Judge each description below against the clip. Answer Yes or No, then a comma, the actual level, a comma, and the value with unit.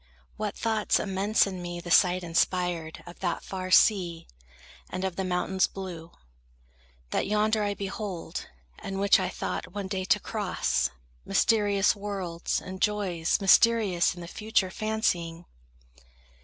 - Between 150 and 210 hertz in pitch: Yes, high, 190 Hz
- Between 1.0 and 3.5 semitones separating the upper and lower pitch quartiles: Yes, average, 2.8 semitones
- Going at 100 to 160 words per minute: Yes, average, 140 wpm